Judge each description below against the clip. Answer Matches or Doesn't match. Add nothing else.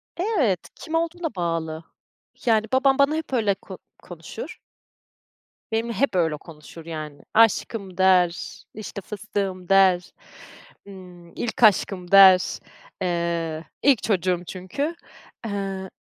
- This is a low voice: Doesn't match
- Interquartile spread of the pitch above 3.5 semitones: Matches